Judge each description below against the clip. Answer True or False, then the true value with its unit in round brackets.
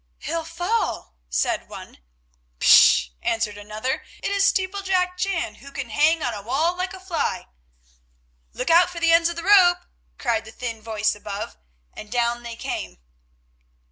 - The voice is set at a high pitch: True (305 Hz)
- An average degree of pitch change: False (8.3 semitones)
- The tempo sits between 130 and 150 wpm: False (160 wpm)